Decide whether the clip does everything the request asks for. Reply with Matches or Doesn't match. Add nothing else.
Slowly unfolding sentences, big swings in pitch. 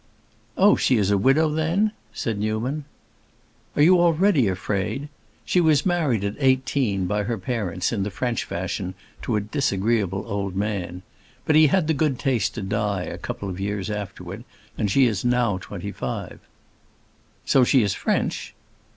Doesn't match